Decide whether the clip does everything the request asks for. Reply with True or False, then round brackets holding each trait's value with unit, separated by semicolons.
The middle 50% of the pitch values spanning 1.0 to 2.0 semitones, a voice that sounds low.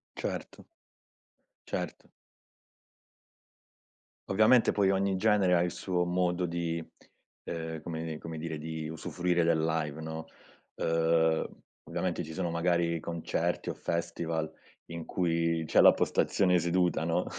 True (1.6 semitones; 85 Hz)